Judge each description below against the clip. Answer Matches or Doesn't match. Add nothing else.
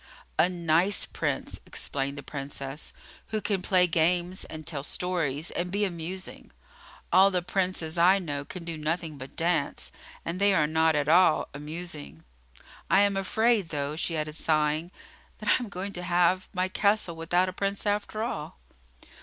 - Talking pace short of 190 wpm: Matches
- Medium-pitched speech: Matches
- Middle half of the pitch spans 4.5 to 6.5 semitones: Doesn't match